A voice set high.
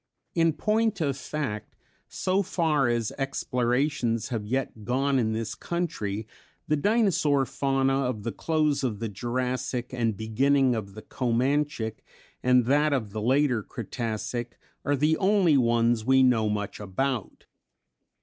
No: low, 130 Hz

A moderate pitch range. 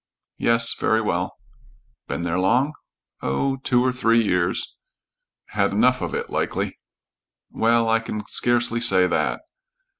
Yes: average, 3.9 semitones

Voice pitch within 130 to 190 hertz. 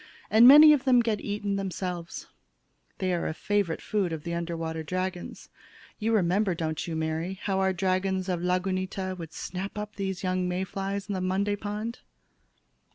Yes: medium, 185 Hz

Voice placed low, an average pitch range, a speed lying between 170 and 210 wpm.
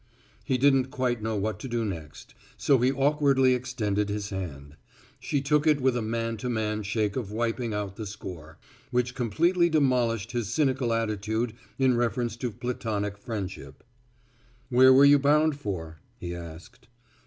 No: low, 115 Hz; average, 4.1 semitones; average, 160 wpm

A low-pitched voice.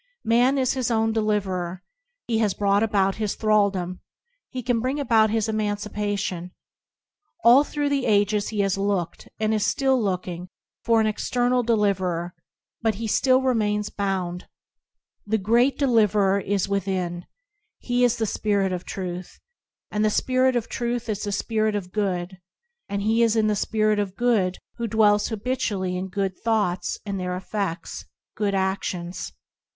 No: high, 210 Hz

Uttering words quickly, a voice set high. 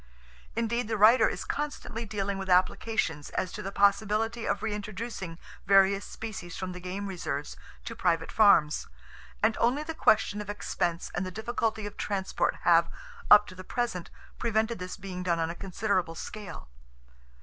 No: average, 160 wpm; high, 200 Hz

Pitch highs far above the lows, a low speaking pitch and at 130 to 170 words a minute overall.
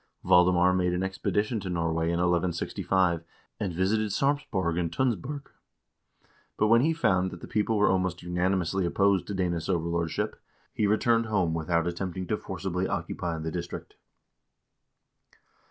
No: average, 3.1 semitones; very low, 90 Hz; average, 140 wpm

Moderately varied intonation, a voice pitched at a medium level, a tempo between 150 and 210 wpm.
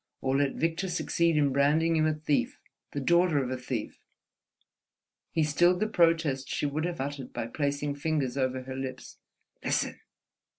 Yes: average, 3.6 semitones; medium, 145 Hz; average, 165 wpm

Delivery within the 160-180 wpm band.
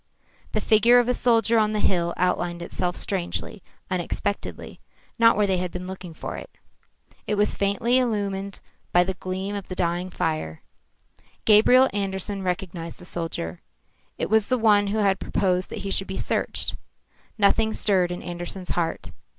Yes: average, 165 wpm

